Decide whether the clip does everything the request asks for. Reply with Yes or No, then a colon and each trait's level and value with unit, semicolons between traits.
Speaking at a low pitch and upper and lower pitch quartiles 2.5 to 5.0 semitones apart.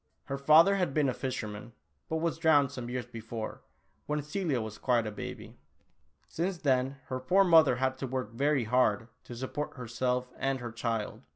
Yes: low, 130 Hz; average, 3.9 semitones